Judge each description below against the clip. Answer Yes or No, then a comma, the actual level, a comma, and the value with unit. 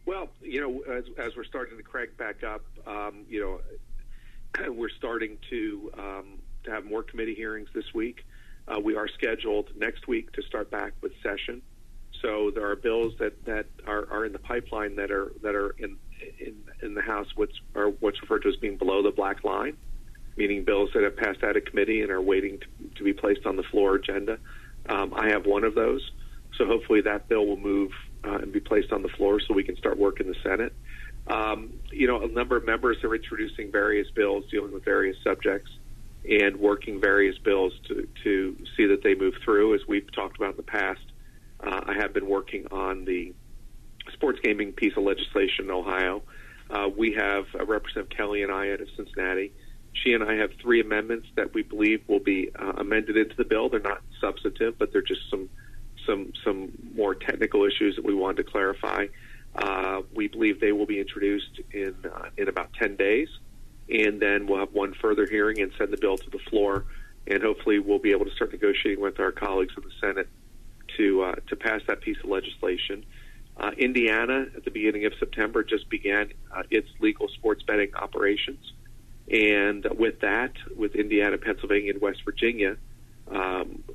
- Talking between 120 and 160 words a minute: No, average, 200 wpm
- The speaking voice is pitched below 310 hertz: No, very high, 330 Hz